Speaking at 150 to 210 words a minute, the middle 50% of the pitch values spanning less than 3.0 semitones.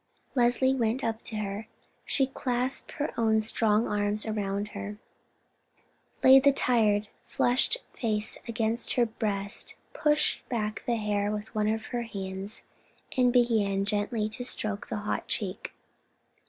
No: average, 140 wpm; narrow, 2.6 semitones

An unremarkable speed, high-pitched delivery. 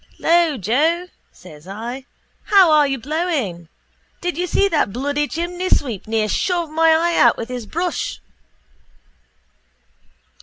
No: slow, 125 wpm; very high, 295 Hz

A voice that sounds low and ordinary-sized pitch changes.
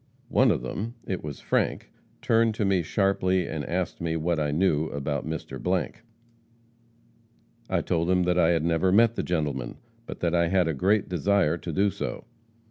Yes: very low, 90 Hz; average, 3.4 semitones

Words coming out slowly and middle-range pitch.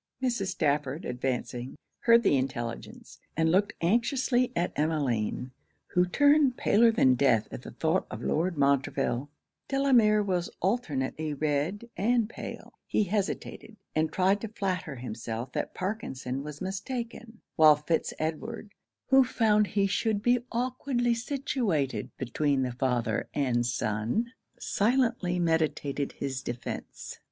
Yes: slow, 125 wpm; medium, 175 Hz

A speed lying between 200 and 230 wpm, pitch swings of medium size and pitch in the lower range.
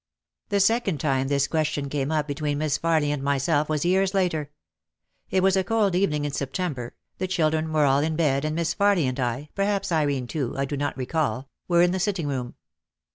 No: fast, 205 wpm; average, 4.3 semitones; medium, 155 Hz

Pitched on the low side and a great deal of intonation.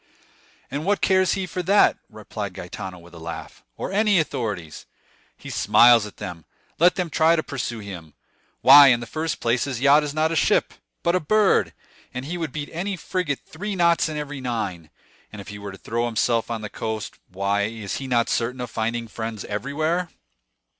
Yes: low, 125 Hz; wide, 7.2 semitones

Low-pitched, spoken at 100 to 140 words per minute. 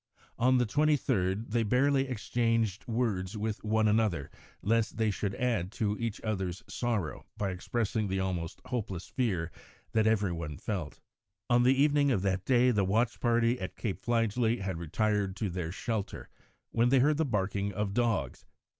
No: low, 110 Hz; average, 165 wpm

